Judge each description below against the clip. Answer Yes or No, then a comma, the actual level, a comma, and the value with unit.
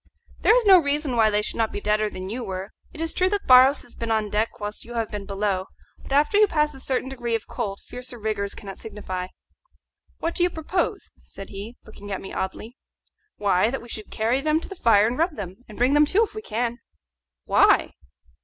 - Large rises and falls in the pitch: Yes, wide, 5.9 semitones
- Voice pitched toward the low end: No, high, 230 Hz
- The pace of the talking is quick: Yes, fast, 225 wpm